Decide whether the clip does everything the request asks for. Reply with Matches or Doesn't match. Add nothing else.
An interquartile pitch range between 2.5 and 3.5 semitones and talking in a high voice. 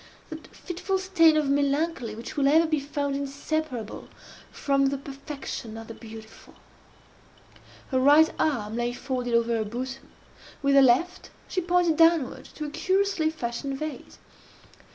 Doesn't match